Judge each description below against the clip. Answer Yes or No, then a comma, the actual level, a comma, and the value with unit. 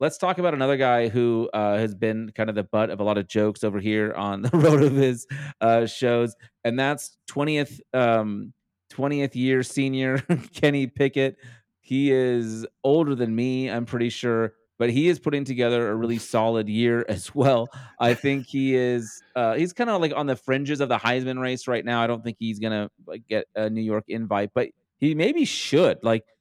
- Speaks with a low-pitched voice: Yes, low, 120 Hz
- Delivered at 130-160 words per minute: No, fast, 205 wpm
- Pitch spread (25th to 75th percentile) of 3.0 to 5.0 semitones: Yes, average, 3.4 semitones